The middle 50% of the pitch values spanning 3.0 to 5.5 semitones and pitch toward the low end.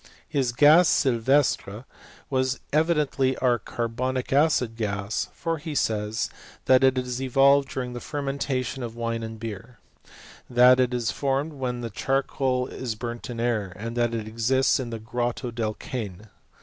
No: narrow, 2.6 semitones; low, 125 Hz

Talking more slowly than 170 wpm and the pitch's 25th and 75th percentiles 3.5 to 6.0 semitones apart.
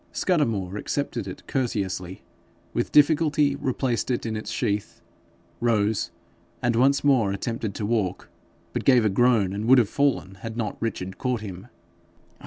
Yes: average, 150 wpm; average, 4.4 semitones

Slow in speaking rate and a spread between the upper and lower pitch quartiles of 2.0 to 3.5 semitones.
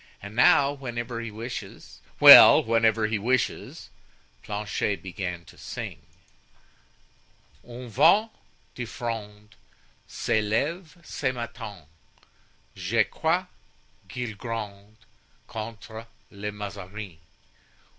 Yes: slow, 95 wpm; average, 2.7 semitones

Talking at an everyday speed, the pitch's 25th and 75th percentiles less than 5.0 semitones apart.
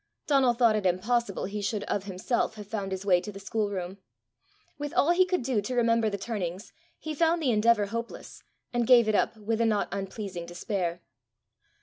Yes: average, 195 wpm; average, 3.4 semitones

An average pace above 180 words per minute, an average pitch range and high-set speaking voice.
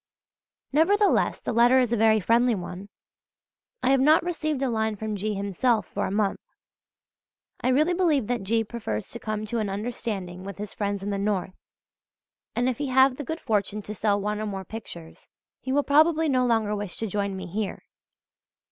Yes: average, 190 wpm; average, 4.2 semitones; high, 220 Hz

